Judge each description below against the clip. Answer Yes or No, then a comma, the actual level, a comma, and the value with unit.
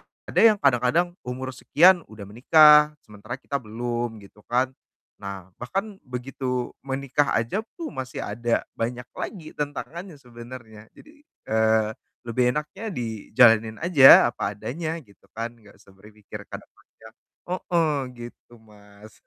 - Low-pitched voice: Yes, low, 120 Hz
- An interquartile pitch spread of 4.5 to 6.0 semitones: Yes, average, 5.0 semitones